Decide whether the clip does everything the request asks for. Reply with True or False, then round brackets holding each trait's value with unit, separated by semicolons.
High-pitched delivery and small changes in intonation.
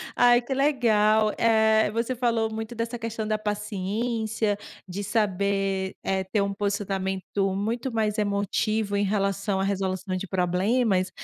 True (210 Hz; 2.3 semitones)